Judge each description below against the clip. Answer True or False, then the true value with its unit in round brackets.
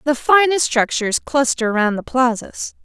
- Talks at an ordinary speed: True (150 wpm)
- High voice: True (260 Hz)